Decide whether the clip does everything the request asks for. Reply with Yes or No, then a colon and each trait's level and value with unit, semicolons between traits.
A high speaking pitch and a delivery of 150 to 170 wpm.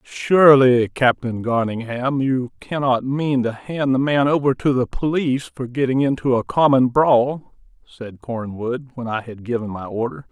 No: low, 130 Hz; average, 165 wpm